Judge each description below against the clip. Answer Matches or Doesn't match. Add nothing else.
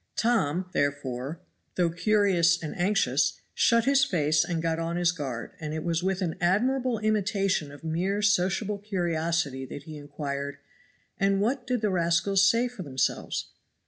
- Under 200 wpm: Matches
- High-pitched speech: Doesn't match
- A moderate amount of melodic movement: Matches